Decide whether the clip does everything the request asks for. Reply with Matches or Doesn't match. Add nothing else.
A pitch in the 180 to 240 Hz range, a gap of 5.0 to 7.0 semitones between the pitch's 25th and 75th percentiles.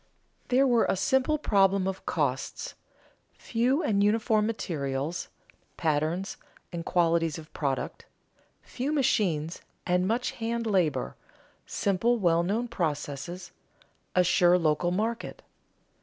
Matches